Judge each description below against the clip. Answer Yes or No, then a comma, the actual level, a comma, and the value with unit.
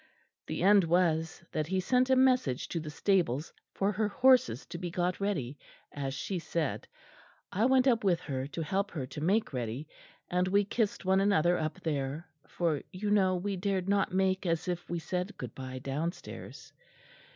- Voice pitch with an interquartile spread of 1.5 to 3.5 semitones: No, average, 4.5 semitones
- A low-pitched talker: No, medium, 180 Hz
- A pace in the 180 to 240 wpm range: Yes, average, 185 wpm